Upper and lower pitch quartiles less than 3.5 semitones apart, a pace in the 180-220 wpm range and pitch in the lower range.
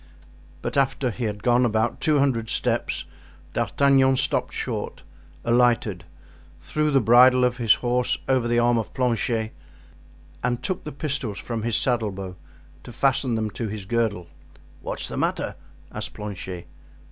No: average, 3.0 semitones; average, 150 wpm; low, 120 Hz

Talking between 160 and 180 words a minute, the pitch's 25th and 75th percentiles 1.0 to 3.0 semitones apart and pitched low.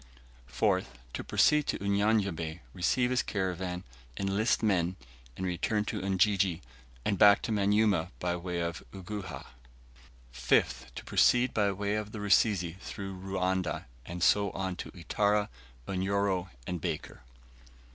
No: slow, 135 wpm; narrow, 2.4 semitones; very low, 95 Hz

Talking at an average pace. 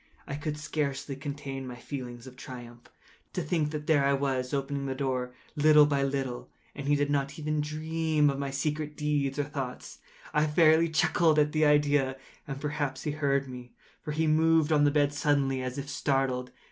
Yes: average, 190 wpm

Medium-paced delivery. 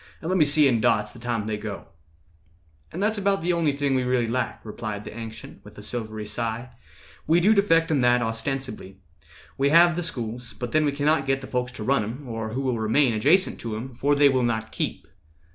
No: fast, 220 wpm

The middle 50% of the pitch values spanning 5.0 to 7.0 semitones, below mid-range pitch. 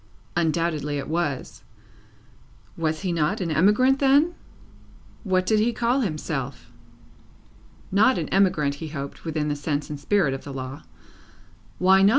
No: wide, 5.4 semitones; medium, 165 Hz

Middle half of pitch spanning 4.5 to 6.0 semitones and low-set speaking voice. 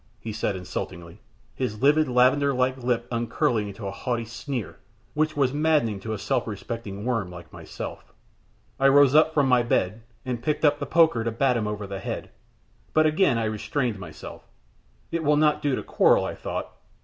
Yes: average, 4.9 semitones; low, 120 Hz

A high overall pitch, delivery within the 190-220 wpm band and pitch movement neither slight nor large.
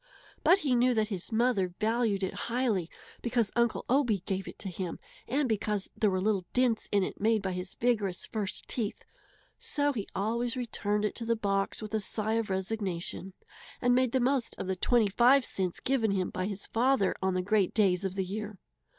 Yes: high, 215 Hz; average, 200 wpm; average, 3.8 semitones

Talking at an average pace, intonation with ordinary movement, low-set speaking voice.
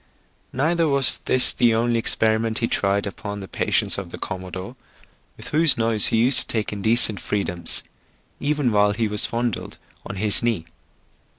Yes: average, 165 wpm; average, 3.0 semitones; low, 110 Hz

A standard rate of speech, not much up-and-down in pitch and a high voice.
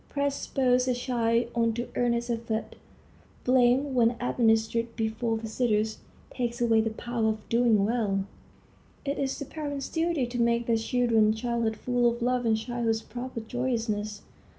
Yes: average, 150 wpm; narrow, 1.8 semitones; high, 235 Hz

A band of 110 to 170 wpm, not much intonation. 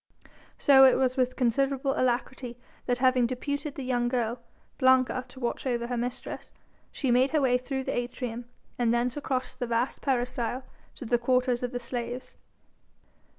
Yes: average, 165 wpm; narrow, 1.4 semitones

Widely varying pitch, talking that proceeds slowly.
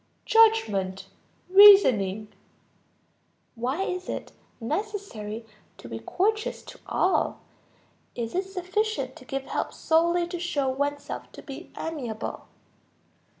Yes: wide, 8.7 semitones; slow, 105 wpm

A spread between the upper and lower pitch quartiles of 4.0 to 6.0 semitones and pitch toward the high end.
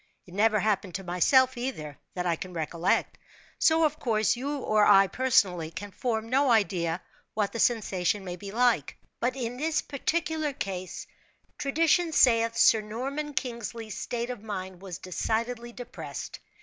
Yes: average, 5.2 semitones; high, 225 Hz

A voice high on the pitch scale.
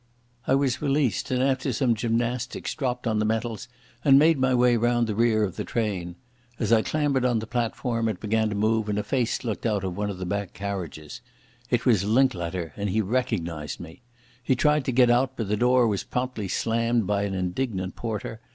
No: low, 115 Hz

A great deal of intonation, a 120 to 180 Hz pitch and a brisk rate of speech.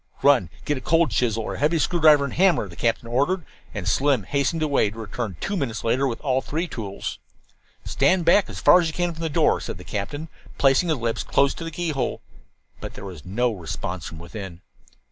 Yes: wide, 6.6 semitones; low, 135 Hz; fast, 215 wpm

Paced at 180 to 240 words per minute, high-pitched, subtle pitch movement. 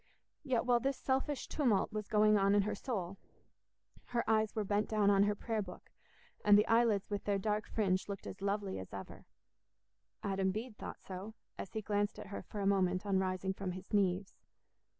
Yes: average, 195 wpm; high, 205 Hz; narrow, 2.0 semitones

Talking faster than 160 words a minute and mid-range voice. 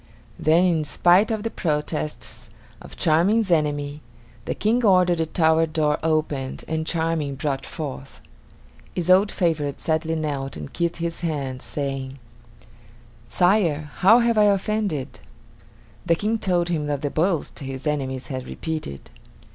No: average, 140 wpm; medium, 160 Hz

